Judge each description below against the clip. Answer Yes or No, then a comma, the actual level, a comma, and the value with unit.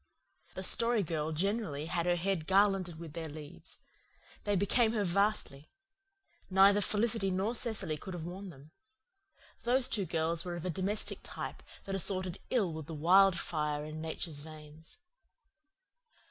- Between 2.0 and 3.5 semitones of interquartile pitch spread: No, average, 4.0 semitones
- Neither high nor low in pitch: Yes, medium, 180 Hz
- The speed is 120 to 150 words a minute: Yes, average, 145 wpm